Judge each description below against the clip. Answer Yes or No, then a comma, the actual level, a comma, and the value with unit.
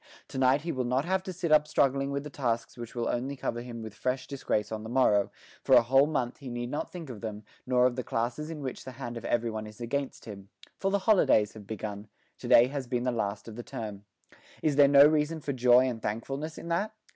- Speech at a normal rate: No, fast, 250 wpm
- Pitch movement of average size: Yes, average, 3.7 semitones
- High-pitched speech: No, low, 125 Hz